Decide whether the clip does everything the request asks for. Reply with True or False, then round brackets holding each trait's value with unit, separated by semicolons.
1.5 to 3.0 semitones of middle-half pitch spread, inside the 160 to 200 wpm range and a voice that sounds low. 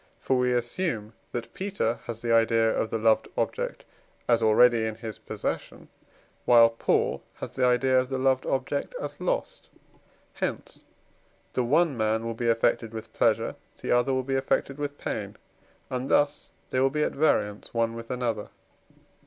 True (2.7 semitones; 170 wpm; 120 Hz)